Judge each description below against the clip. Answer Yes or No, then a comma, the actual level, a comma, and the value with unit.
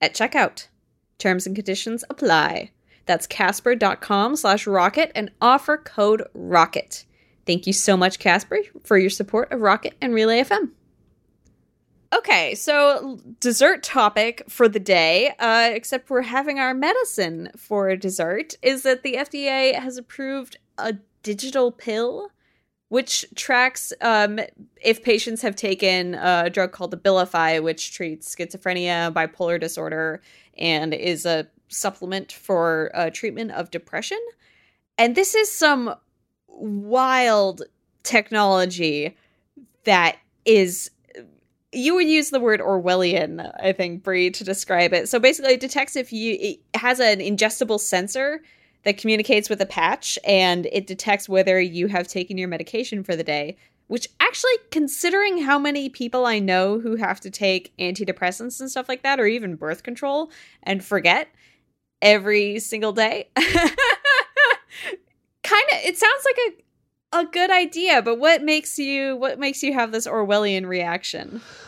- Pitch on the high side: Yes, high, 220 Hz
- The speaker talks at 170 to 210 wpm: No, average, 145 wpm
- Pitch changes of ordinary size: No, wide, 6.0 semitones